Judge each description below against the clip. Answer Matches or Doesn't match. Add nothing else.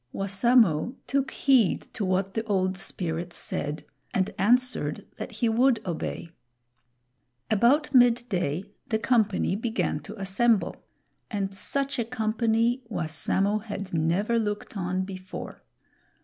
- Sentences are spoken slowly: Matches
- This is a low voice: Doesn't match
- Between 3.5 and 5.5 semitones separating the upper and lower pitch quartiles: Matches